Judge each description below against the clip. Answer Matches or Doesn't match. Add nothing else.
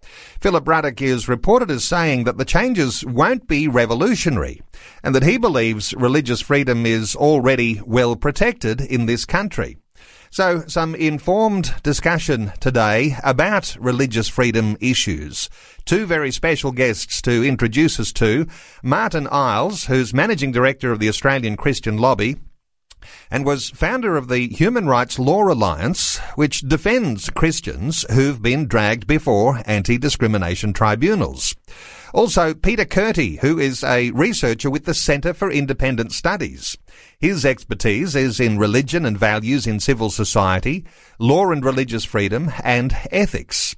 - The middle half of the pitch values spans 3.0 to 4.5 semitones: Doesn't match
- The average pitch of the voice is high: Doesn't match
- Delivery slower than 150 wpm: Matches